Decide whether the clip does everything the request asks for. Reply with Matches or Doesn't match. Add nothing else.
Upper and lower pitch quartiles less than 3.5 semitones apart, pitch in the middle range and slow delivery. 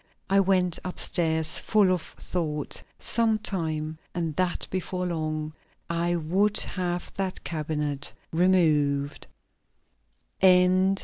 Matches